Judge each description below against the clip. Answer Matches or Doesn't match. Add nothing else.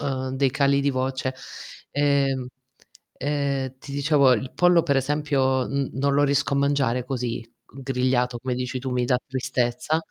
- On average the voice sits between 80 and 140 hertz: Matches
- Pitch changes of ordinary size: Doesn't match